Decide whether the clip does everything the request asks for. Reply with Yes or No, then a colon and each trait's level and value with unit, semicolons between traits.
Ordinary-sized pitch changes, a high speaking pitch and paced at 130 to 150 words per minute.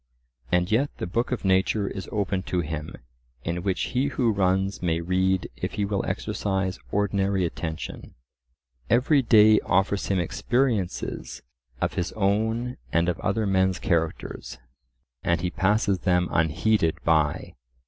No: average, 3.2 semitones; very low, 95 Hz; average, 140 wpm